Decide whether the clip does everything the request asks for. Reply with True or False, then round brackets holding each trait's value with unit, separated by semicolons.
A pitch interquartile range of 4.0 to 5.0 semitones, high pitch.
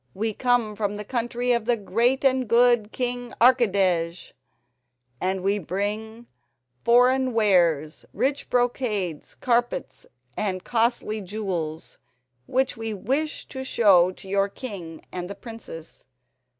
True (4.3 semitones; 220 Hz)